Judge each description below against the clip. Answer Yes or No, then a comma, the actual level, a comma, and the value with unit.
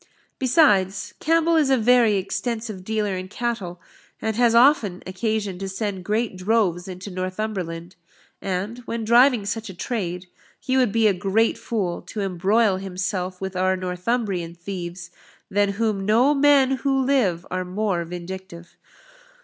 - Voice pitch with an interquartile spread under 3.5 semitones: No, average, 4.0 semitones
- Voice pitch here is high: Yes, high, 200 Hz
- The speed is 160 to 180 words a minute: No, average, 145 wpm